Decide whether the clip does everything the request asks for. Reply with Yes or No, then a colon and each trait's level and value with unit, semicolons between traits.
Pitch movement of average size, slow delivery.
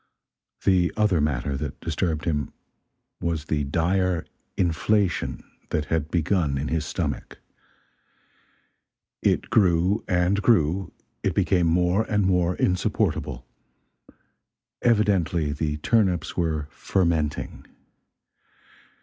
Yes: average, 3.5 semitones; slow, 100 wpm